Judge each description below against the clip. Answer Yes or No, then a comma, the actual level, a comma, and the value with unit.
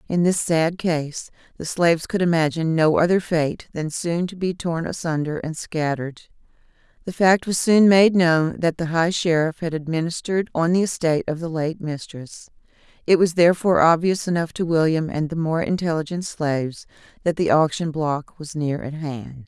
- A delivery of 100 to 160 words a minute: No, average, 180 wpm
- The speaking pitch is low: No, medium, 165 Hz